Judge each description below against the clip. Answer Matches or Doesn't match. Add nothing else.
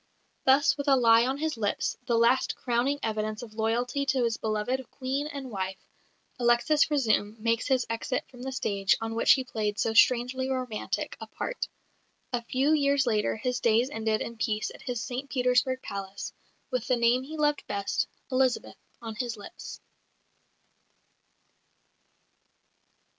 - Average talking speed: Matches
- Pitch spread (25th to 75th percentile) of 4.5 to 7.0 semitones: Doesn't match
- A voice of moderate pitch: Doesn't match